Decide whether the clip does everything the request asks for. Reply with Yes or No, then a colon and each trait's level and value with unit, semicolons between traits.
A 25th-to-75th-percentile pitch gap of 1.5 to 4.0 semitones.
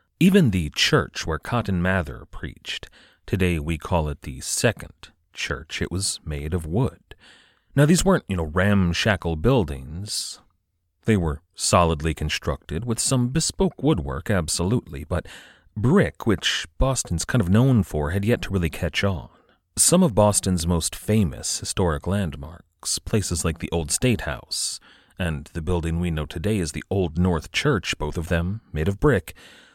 No: average, 4.5 semitones